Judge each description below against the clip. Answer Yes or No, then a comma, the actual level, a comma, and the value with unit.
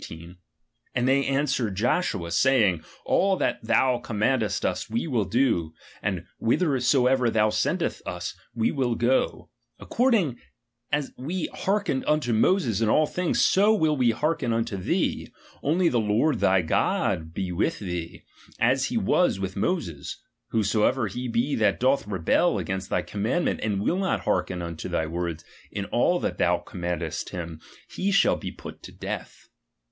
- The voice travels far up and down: Yes, wide, 7.1 semitones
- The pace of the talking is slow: No, average, 165 wpm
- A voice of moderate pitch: No, low, 115 Hz